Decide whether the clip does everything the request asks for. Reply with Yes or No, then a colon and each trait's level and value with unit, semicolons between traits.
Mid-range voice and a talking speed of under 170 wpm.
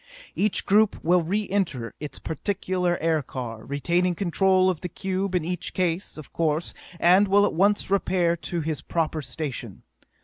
Yes: medium, 175 Hz; average, 160 wpm